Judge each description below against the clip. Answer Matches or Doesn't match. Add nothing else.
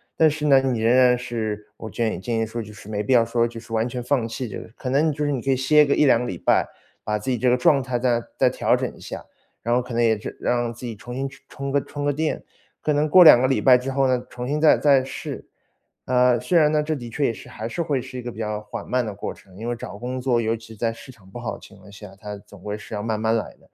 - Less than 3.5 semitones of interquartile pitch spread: Matches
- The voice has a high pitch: Doesn't match